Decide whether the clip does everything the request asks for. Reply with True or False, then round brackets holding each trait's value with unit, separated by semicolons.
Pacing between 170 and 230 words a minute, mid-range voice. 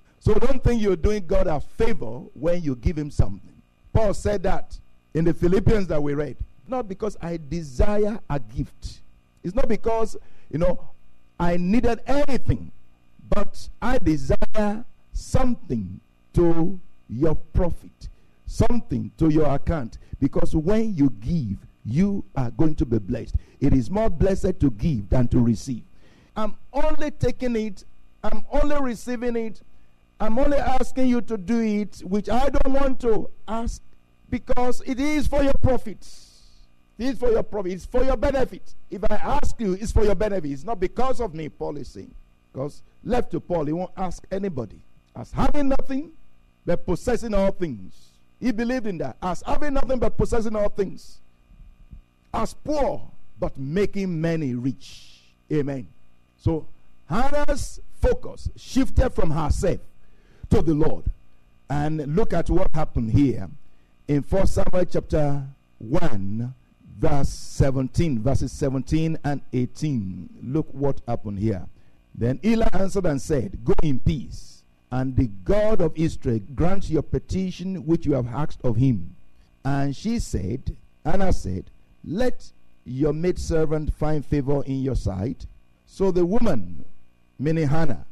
False (150 wpm; 160 Hz)